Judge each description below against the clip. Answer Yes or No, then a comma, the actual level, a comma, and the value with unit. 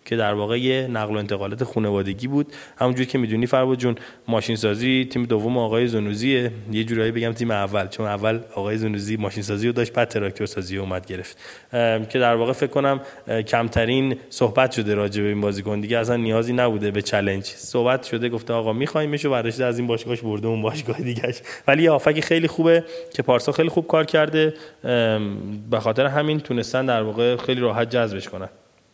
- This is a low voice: Yes, low, 115 Hz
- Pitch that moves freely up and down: No, average, 3.4 semitones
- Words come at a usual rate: No, fast, 185 wpm